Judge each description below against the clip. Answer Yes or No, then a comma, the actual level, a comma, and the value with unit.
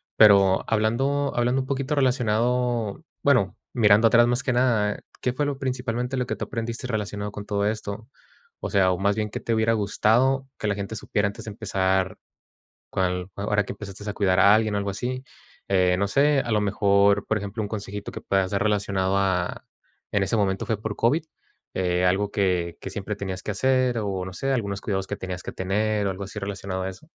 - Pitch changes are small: No, average, 3.3 semitones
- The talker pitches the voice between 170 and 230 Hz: No, low, 105 Hz